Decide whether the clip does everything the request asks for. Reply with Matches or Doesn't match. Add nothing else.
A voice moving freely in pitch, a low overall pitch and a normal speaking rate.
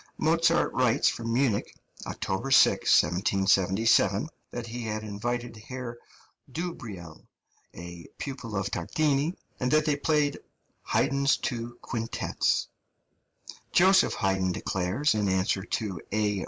Doesn't match